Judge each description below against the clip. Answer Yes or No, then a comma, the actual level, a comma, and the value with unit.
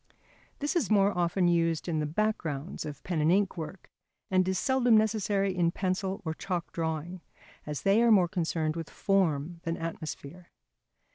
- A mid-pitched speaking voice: Yes, medium, 175 Hz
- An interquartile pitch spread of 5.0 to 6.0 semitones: No, average, 3.4 semitones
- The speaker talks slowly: No, average, 165 wpm